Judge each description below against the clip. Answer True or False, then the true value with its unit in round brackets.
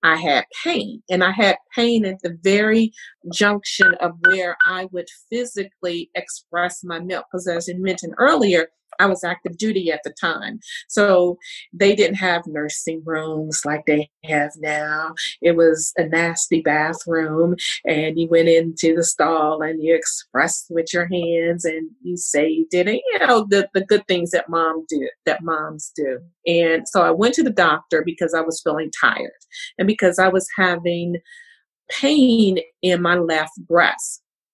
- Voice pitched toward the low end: False (175 Hz)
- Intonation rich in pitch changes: False (3.7 semitones)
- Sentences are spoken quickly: False (165 wpm)